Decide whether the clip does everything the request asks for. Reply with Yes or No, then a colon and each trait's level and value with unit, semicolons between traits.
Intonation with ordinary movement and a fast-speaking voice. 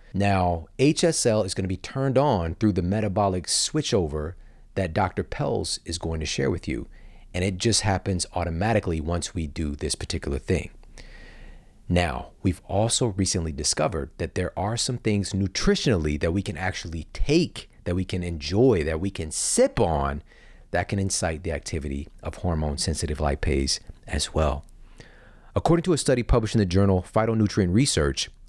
No: average, 4.7 semitones; average, 165 wpm